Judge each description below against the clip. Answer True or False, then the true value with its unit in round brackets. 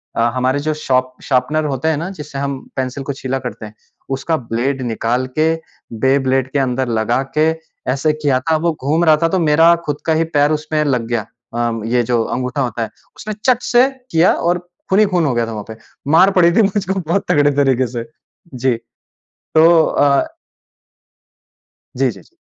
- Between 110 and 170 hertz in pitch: True (140 Hz)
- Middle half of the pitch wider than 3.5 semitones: True (3.9 semitones)